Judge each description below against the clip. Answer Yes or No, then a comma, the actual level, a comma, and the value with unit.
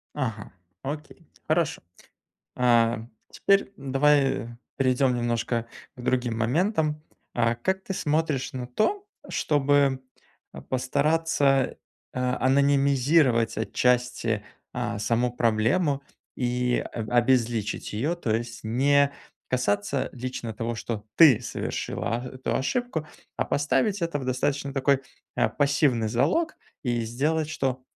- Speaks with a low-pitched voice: Yes, low, 130 Hz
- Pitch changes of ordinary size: Yes, average, 3.6 semitones